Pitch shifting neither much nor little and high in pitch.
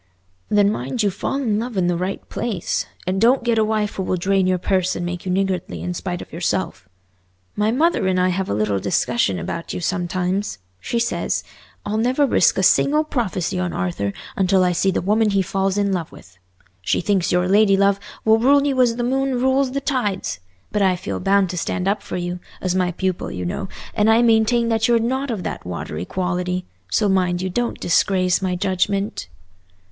Yes: average, 3.7 semitones; high, 195 Hz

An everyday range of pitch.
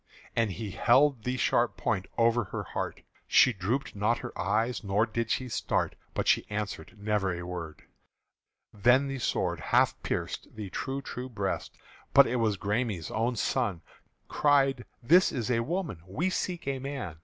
Yes: average, 4.5 semitones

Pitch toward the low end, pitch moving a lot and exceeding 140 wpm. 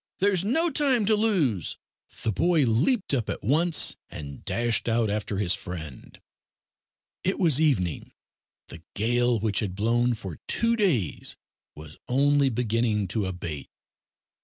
No: low, 120 Hz; wide, 8.7 semitones; slow, 135 wpm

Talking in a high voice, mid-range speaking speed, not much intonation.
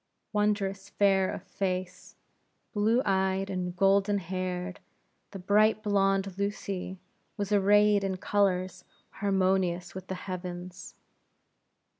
No: high, 195 Hz; slow, 105 wpm; narrow, 1.6 semitones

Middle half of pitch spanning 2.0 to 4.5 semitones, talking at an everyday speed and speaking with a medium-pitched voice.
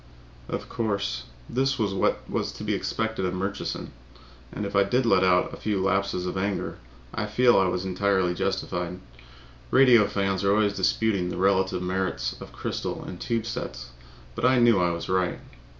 No: average, 2.9 semitones; average, 180 wpm; low, 100 Hz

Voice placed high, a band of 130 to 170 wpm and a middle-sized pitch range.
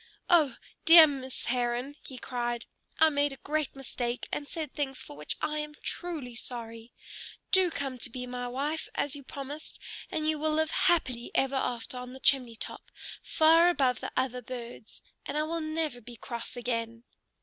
No: very high, 265 Hz; average, 185 wpm; average, 3.9 semitones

